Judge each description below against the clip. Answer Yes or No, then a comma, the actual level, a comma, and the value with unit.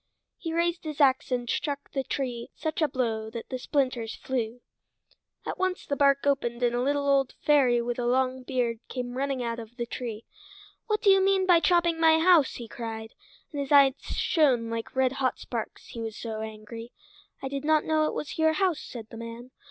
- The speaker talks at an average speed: No, fast, 210 wpm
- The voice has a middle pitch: No, very high, 260 Hz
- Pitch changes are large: No, average, 4.2 semitones